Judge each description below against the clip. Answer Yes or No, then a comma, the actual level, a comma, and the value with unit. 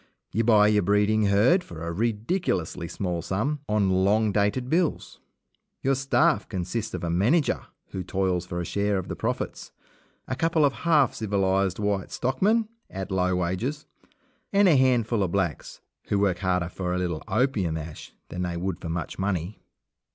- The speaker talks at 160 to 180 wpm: Yes, average, 170 wpm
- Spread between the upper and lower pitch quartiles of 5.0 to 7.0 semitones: Yes, average, 5.3 semitones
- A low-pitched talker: Yes, low, 100 Hz